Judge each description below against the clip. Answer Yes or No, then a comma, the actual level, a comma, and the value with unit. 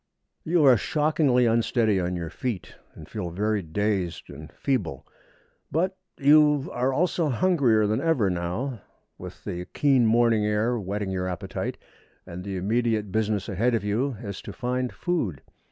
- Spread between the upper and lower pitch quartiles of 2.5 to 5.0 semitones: No, wide, 5.5 semitones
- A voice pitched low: Yes, low, 110 Hz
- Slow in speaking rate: No, average, 155 wpm